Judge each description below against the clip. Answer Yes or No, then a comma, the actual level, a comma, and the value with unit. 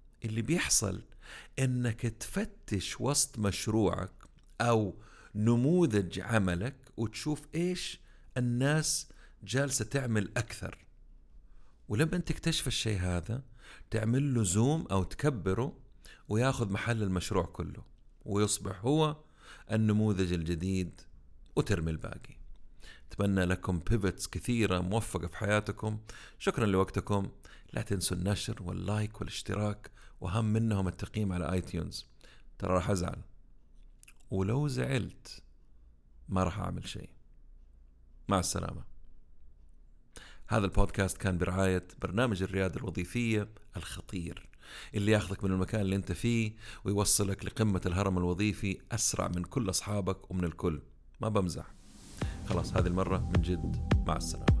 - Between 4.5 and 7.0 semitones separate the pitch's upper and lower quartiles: No, average, 3.9 semitones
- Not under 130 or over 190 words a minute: No, average, 110 wpm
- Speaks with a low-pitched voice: Yes, low, 100 Hz